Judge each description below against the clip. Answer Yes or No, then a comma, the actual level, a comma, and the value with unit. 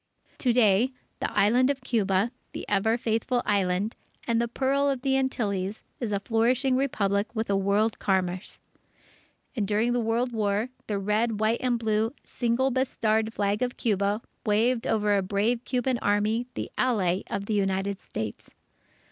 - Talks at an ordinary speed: Yes, average, 155 wpm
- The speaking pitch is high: Yes, high, 220 Hz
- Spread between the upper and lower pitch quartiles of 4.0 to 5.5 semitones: No, average, 3.3 semitones